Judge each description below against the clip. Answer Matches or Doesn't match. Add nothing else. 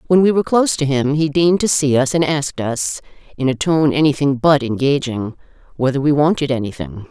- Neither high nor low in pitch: Matches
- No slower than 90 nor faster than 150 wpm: Doesn't match